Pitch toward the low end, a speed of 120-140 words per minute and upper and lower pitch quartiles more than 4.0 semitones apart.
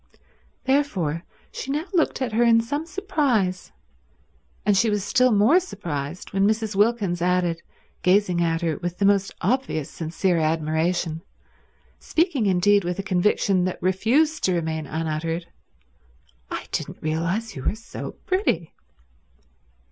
No: high, 190 Hz; slow, 135 wpm; wide, 5.4 semitones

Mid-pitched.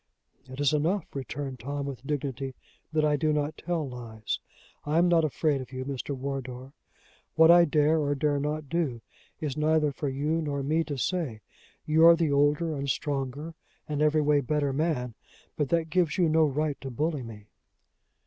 Yes: medium, 145 Hz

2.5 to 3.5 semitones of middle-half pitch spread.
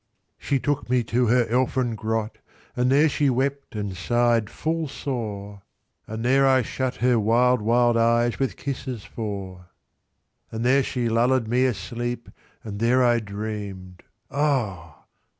Yes: average, 3.1 semitones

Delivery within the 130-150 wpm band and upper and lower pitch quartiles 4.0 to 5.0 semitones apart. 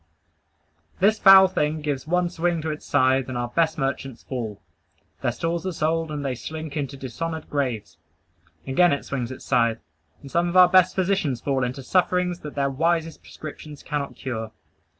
No: average, 175 wpm; average, 4.5 semitones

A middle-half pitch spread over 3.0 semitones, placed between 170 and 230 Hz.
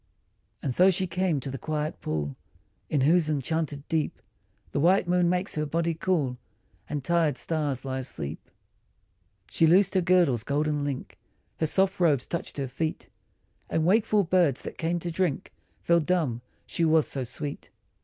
No: average, 3.9 semitones; medium, 160 Hz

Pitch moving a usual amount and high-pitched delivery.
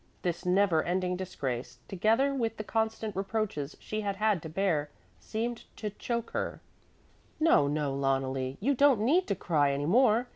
No: wide, 6.9 semitones; high, 195 Hz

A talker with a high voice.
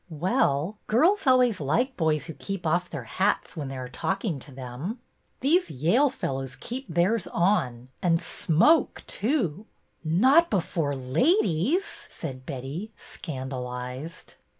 No: medium, 170 Hz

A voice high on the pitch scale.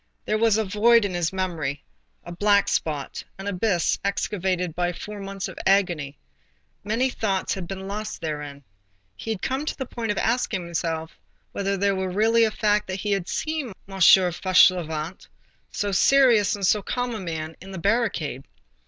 Yes: high, 195 Hz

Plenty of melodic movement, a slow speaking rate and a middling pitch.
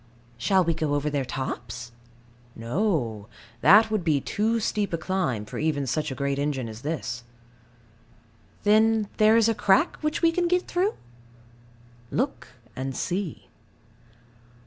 No: wide, 8.2 semitones; average, 145 wpm; medium, 165 Hz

